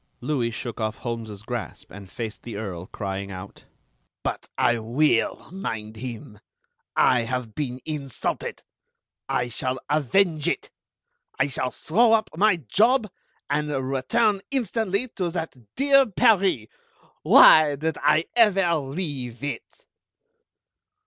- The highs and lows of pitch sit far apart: Yes, wide, 8.3 semitones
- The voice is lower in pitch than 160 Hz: Yes, medium, 140 Hz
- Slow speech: Yes, slow, 120 wpm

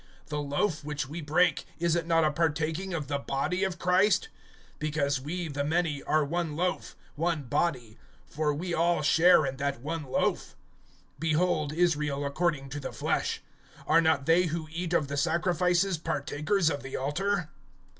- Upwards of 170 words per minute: No, average, 165 wpm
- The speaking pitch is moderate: Yes, medium, 160 Hz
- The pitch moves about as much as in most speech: Yes, average, 3.1 semitones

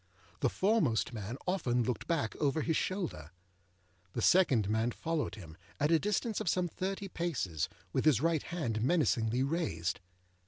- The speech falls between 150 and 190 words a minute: Yes, average, 155 wpm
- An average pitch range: No, wide, 7.6 semitones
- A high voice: No, medium, 145 Hz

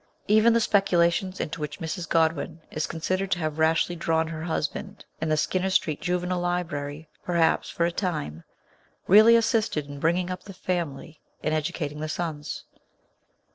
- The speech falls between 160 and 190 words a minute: Yes, average, 165 wpm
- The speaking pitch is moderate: Yes, medium, 165 Hz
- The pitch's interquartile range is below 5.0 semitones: Yes, average, 2.8 semitones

